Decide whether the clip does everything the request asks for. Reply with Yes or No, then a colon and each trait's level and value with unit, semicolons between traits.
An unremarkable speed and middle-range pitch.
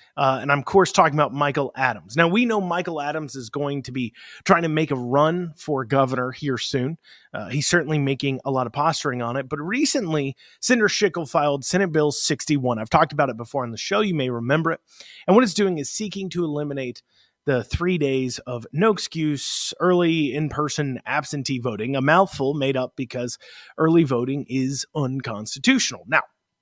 Yes: average, 195 wpm; medium, 145 Hz